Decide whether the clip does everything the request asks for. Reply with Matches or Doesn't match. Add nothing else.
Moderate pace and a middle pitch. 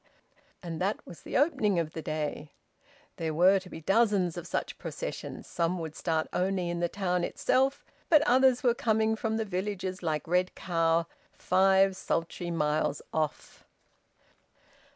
Matches